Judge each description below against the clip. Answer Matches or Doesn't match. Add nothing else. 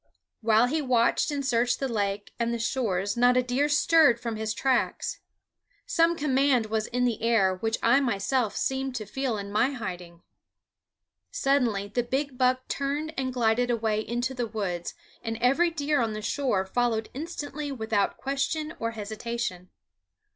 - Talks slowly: Doesn't match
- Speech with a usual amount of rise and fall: Matches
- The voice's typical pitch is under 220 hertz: Doesn't match